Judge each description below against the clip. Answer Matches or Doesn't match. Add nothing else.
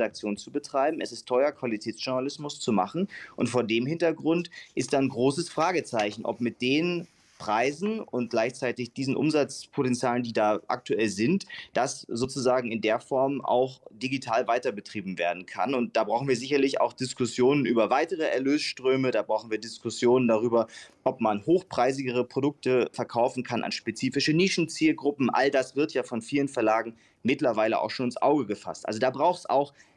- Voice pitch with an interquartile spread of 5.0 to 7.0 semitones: Doesn't match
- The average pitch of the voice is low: Matches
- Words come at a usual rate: Matches